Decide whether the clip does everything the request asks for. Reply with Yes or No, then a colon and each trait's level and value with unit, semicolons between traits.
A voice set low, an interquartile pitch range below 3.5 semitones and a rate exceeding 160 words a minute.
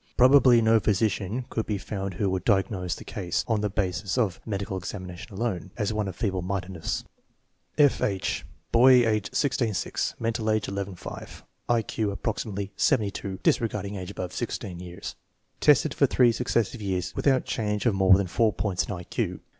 Yes: low, 105 Hz; average, 3.1 semitones; average, 180 wpm